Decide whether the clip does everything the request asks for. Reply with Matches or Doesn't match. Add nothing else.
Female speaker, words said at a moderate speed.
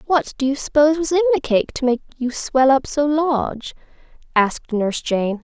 Matches